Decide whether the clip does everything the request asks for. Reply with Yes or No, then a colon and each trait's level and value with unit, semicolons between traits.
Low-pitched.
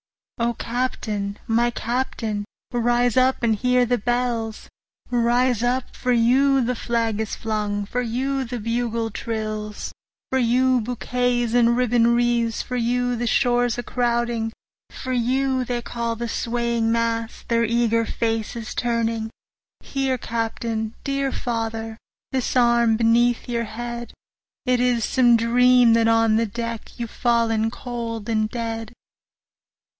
No: high, 235 Hz